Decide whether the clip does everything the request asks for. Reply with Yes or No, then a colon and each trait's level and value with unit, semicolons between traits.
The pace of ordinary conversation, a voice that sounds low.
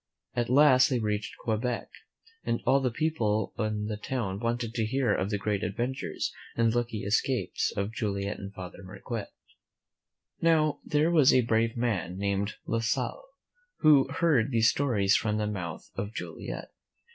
Yes: average, 160 wpm; low, 115 Hz